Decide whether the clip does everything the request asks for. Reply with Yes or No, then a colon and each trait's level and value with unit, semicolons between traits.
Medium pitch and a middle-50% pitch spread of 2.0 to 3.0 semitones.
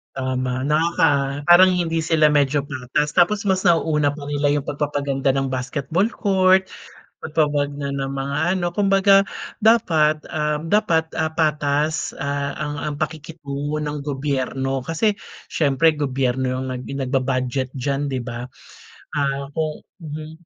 Yes: medium, 145 Hz; average, 2.7 semitones